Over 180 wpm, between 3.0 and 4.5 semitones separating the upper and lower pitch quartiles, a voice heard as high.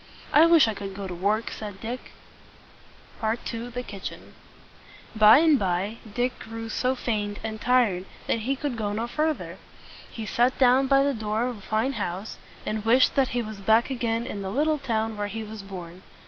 Yes: average, 190 wpm; average, 3.4 semitones; high, 225 Hz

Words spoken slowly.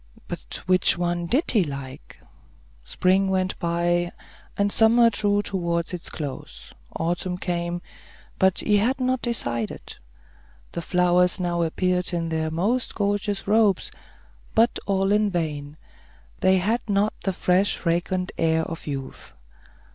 Yes: slow, 130 wpm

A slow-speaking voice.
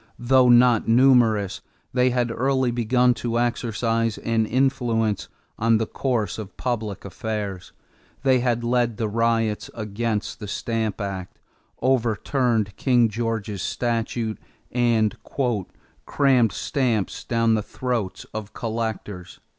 Yes: slow, 115 wpm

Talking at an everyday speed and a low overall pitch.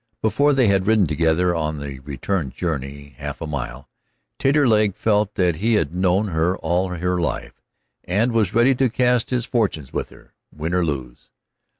Yes: average, 175 wpm; very low, 90 Hz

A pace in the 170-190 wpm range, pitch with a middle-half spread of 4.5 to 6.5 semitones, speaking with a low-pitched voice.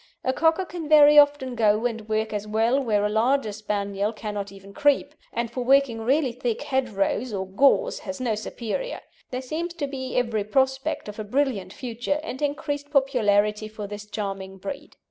No: average, 180 wpm; average, 4.9 semitones; high, 240 Hz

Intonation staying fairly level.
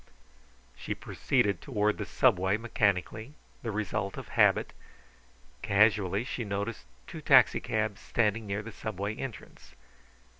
Yes: narrow, 1.9 semitones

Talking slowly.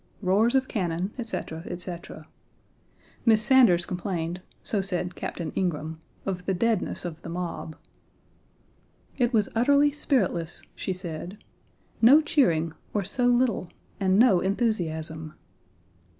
Yes: slow, 120 wpm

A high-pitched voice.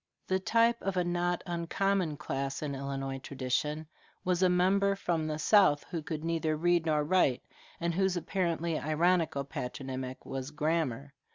No: medium, 160 Hz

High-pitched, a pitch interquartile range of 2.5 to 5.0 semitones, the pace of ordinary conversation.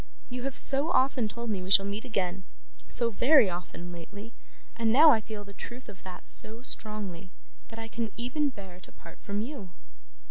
Yes: high, 220 Hz; average, 4.2 semitones; average, 190 wpm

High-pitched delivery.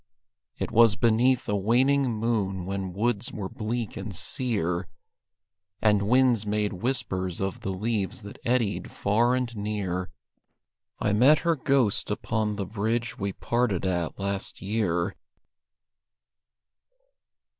No: low, 105 Hz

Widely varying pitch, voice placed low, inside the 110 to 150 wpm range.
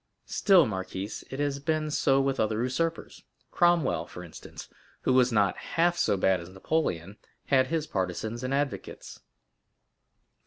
Yes: wide, 7.6 semitones; low, 130 Hz; average, 140 wpm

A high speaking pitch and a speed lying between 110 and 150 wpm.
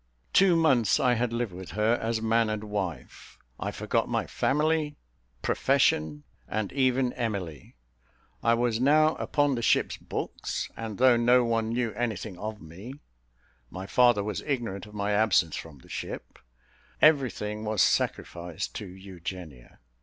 No: low, 110 Hz; average, 145 wpm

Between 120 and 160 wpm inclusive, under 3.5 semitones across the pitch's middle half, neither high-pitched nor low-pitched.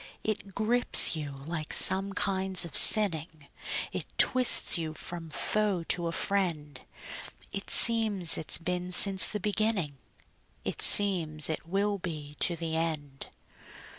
No: slow, 135 wpm; average, 4.0 semitones; medium, 180 Hz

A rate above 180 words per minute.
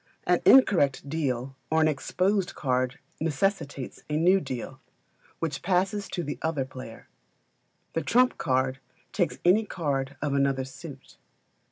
No: slow, 135 wpm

